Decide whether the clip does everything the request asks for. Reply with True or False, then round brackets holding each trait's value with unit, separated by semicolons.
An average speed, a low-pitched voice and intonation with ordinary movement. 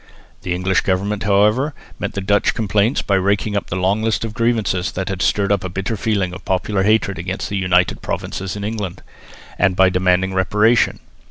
False (190 wpm; 100 Hz; 2.2 semitones)